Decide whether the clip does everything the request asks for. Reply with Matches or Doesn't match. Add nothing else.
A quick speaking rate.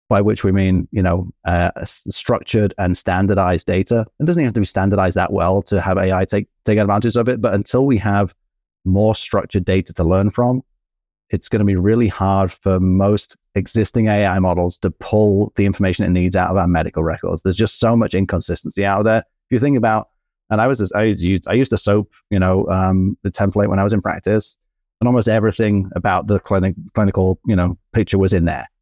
Matches